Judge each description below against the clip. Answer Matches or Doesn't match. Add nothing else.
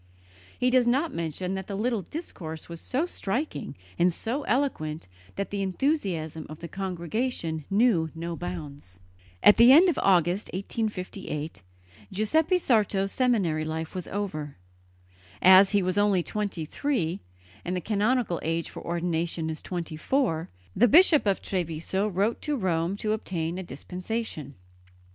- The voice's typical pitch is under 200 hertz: Matches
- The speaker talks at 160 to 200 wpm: Doesn't match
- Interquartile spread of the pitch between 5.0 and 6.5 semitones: Matches